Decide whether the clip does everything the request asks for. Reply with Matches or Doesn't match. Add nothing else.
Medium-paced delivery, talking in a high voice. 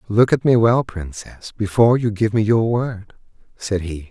Doesn't match